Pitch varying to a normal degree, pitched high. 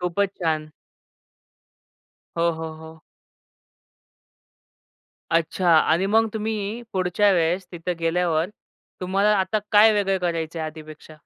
No: average, 3.6 semitones; medium, 180 Hz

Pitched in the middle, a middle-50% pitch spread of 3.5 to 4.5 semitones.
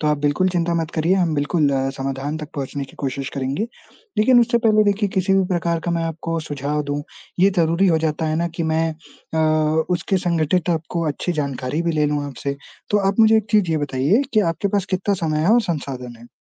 Yes: medium, 160 Hz; average, 4.1 semitones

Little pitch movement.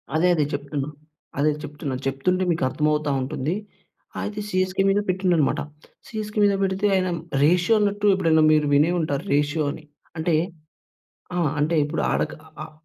No: average, 3.9 semitones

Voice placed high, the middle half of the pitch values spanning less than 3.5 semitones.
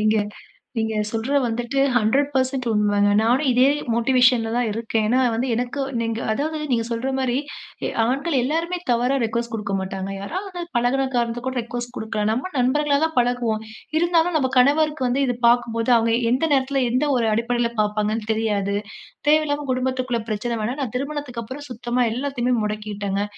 Yes: high, 245 Hz; average, 3.1 semitones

